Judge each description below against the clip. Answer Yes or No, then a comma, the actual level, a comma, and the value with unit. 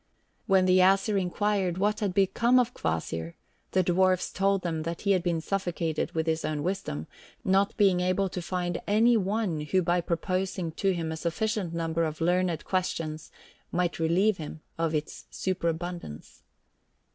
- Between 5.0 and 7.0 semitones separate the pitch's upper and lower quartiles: No, average, 2.9 semitones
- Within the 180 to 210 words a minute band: No, average, 160 wpm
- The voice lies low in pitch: No, medium, 180 Hz